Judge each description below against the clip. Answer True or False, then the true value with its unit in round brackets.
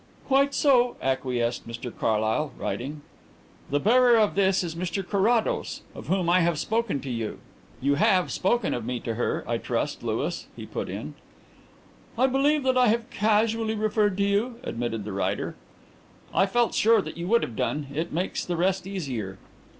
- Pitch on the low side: False (190 Hz)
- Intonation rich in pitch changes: True (9.0 semitones)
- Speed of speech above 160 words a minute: True (175 wpm)